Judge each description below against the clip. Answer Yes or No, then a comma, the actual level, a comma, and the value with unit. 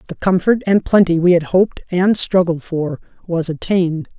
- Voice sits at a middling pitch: Yes, medium, 175 Hz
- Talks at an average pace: Yes, average, 170 wpm